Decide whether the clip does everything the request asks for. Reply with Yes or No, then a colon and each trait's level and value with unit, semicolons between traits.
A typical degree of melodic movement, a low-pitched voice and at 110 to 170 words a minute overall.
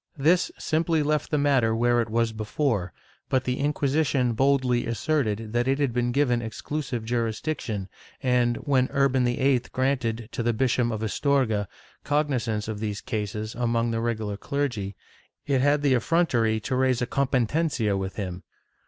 Yes: average, 3.7 semitones; low, 120 Hz; average, 165 wpm